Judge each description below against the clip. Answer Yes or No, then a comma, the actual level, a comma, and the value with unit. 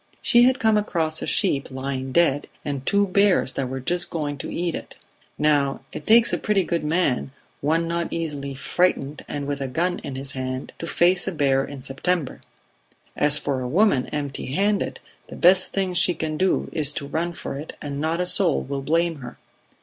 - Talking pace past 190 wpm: Yes, average, 200 wpm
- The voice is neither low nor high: Yes, medium, 155 Hz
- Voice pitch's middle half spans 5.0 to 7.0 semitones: No, average, 4.4 semitones